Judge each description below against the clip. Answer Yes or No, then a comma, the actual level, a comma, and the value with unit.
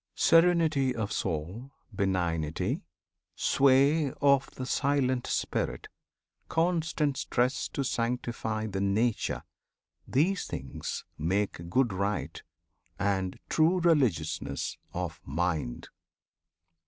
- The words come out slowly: Yes, slow, 90 wpm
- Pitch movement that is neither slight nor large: No, wide, 7.4 semitones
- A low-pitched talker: Yes, low, 120 Hz